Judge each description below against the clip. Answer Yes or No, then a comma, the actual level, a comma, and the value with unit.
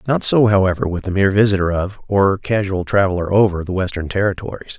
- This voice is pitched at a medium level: No, low, 100 Hz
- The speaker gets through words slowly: No, average, 190 wpm